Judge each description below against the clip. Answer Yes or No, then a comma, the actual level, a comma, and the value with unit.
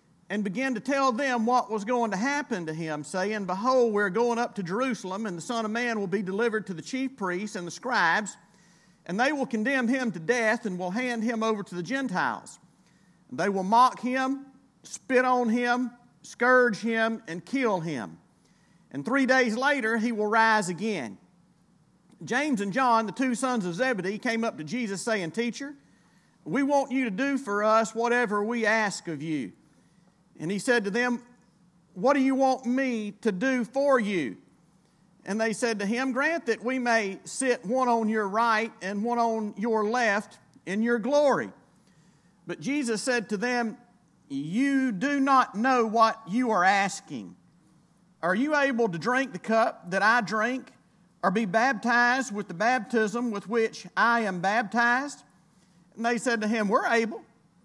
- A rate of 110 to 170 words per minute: No, average, 180 wpm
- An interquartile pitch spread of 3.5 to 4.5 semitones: Yes, average, 4.1 semitones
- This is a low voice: No, high, 225 Hz